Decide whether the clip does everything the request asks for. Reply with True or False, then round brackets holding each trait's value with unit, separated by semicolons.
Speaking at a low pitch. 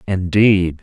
True (95 Hz)